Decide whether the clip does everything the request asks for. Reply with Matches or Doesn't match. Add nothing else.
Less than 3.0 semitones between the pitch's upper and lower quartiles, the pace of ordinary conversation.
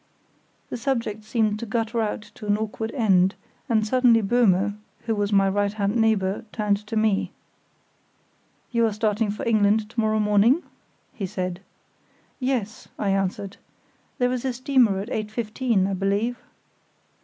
Matches